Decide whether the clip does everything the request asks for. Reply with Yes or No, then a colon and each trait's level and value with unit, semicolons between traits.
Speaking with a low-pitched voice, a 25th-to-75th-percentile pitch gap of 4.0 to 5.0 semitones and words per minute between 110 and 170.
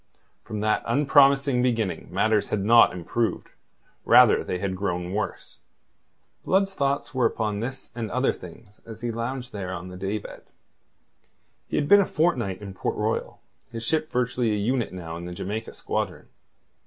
Yes: low, 115 Hz; average, 4.5 semitones; average, 165 wpm